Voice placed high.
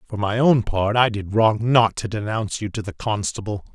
No: low, 110 Hz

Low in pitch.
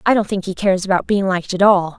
No: high, 190 Hz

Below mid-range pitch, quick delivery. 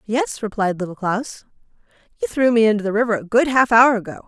No: high, 225 Hz; fast, 210 wpm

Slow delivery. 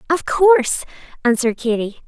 Yes: slow, 115 wpm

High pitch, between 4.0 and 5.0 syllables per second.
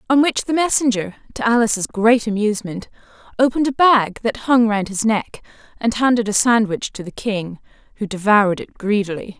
No: high, 220 Hz; 5.4 syllables/s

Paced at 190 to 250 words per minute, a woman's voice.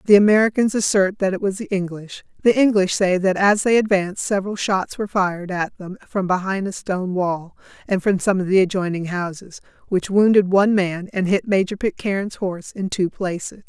Yes: average, 195 wpm; female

